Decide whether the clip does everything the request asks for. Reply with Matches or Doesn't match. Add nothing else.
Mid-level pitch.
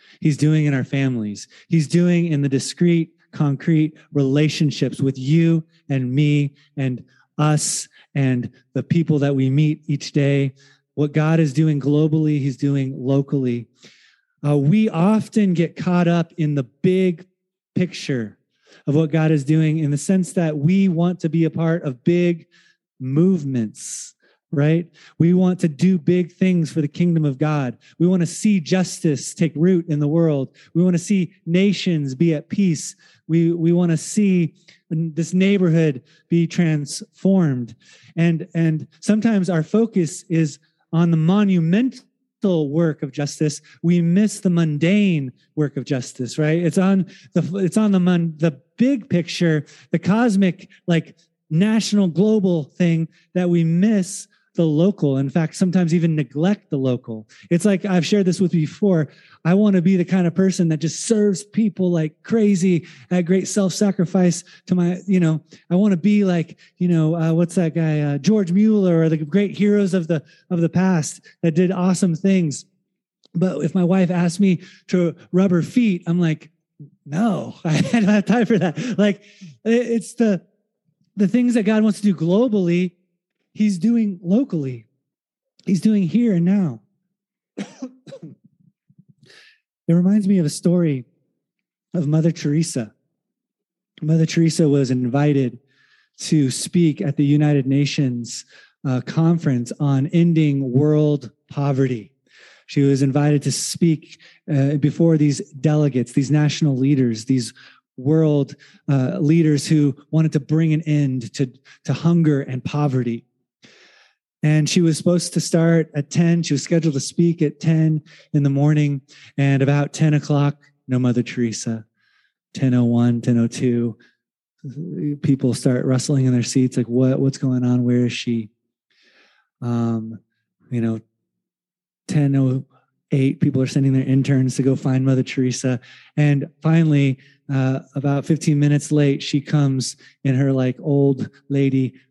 Matches